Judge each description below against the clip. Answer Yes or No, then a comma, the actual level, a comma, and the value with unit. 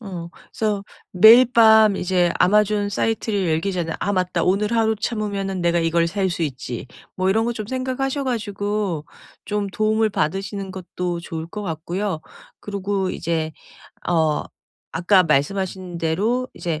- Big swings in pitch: No, average, 3.6 semitones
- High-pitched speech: Yes, high, 195 Hz